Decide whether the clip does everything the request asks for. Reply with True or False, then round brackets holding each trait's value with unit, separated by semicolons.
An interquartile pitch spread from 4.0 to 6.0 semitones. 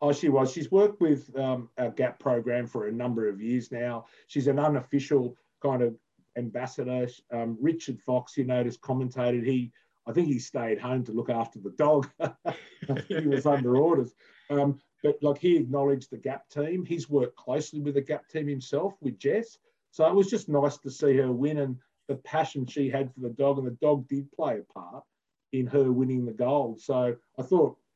False (2.8 semitones)